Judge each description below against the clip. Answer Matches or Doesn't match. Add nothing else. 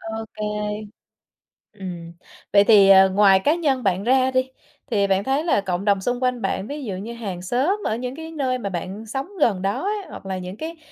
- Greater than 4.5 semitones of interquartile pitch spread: Matches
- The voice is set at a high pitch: Matches